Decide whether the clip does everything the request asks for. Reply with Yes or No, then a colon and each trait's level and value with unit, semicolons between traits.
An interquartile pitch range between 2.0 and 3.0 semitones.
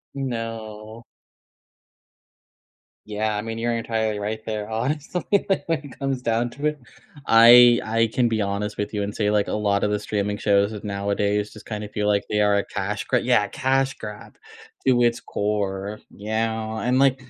Yes: narrow, 2.4 semitones